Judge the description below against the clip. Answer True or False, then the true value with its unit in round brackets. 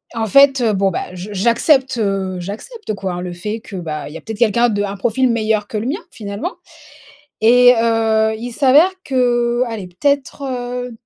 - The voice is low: False (225 Hz)